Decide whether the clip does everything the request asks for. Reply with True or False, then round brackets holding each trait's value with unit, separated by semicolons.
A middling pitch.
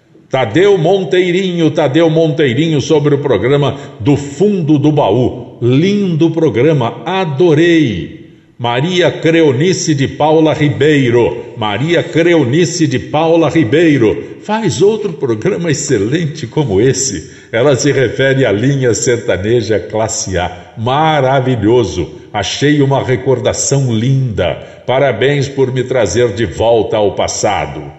True (150 Hz)